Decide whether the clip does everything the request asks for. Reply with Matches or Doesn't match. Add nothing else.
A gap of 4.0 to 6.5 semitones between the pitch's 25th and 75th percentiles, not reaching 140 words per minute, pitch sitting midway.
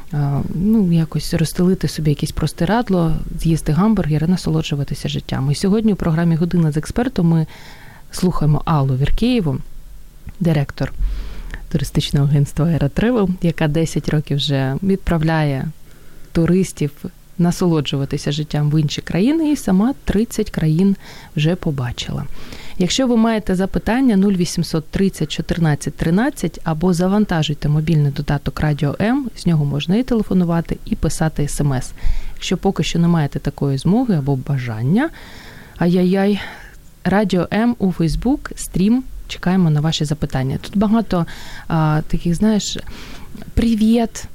Matches